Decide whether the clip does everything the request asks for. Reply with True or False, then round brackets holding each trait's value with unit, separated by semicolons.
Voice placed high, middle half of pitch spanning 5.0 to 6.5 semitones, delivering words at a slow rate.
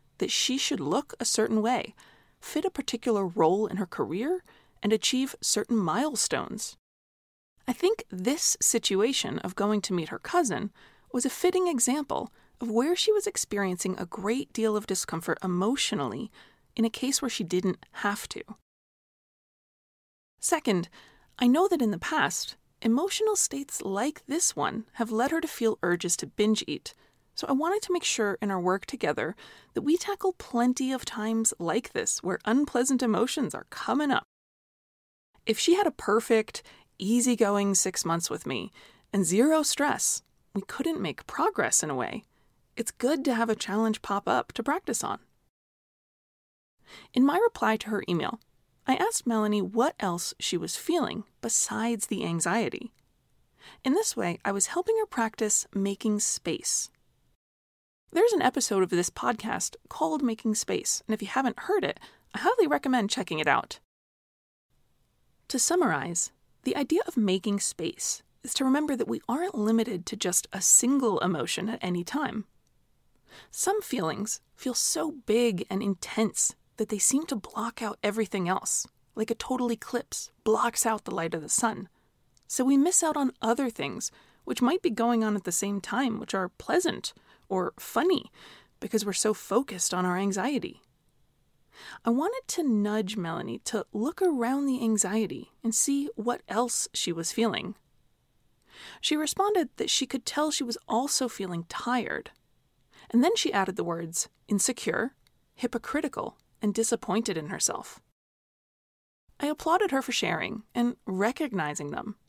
False (230 Hz; 5.3 semitones; 160 wpm)